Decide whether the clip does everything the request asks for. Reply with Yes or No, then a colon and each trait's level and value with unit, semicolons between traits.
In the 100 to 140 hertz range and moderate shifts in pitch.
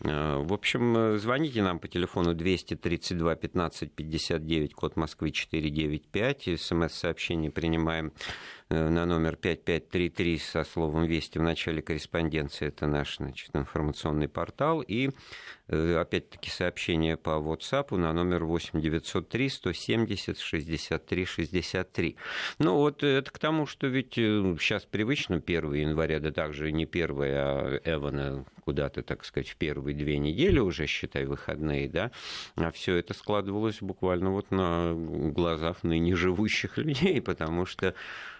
No: very low, 85 Hz; average, 4.1 semitones